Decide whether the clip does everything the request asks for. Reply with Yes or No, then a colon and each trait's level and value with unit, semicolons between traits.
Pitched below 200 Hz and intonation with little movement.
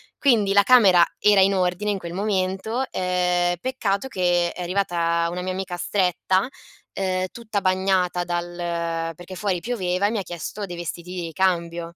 Yes: medium, 185 Hz; narrow, 2.1 semitones